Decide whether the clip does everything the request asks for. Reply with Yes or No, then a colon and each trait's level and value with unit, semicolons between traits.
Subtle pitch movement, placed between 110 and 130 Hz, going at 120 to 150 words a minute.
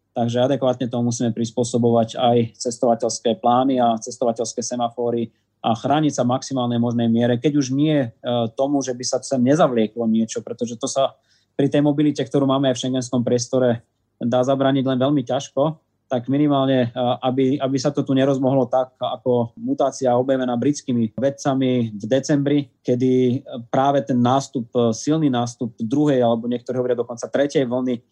No: narrow, 2.2 semitones; low, 125 Hz; average, 160 wpm